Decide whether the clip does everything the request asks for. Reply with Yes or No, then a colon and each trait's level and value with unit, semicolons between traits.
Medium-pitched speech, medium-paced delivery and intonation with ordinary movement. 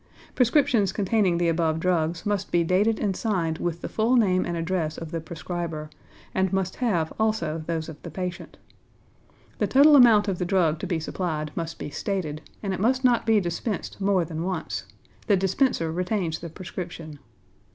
Yes: medium, 180 Hz; average, 180 wpm; average, 4.0 semitones